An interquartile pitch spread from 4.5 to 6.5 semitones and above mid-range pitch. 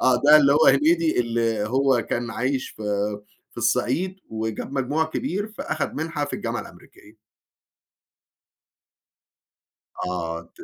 No: average, 5.1 semitones; low, 130 Hz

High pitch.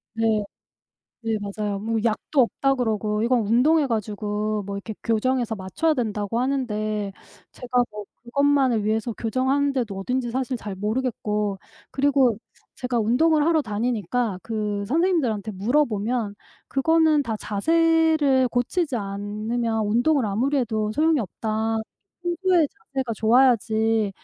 Yes: high, 230 Hz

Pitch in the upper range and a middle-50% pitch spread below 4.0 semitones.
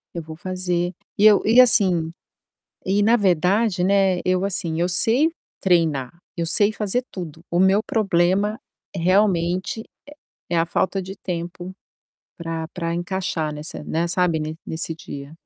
No: medium, 180 Hz; average, 2.9 semitones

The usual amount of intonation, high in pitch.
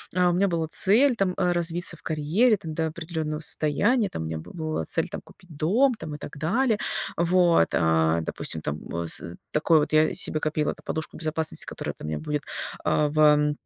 No: average, 3.2 semitones; medium, 160 Hz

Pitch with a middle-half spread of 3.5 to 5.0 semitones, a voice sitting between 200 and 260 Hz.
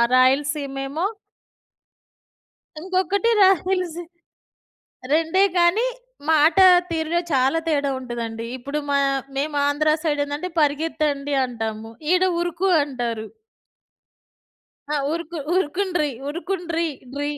No: average, 3.8 semitones; very high, 300 Hz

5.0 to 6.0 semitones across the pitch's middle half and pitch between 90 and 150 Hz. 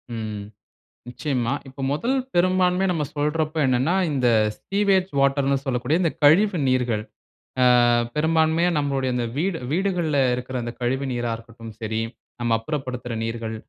Yes: average, 5.3 semitones; medium, 140 Hz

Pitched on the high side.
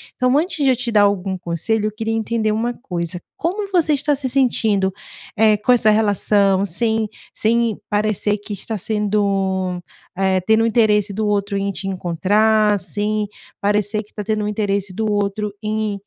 Yes: high, 210 Hz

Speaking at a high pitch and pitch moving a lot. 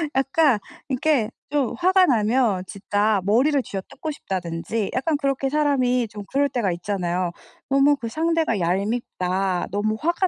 Yes: high, 240 Hz; wide, 6.3 semitones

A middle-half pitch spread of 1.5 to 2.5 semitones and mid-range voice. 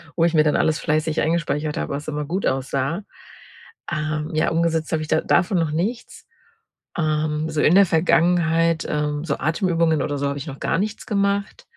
Yes: narrow, 2.0 semitones; medium, 155 Hz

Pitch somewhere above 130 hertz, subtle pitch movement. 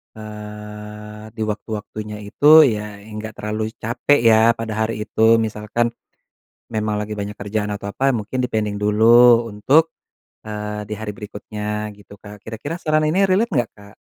No: low, 110 Hz; narrow, 1.5 semitones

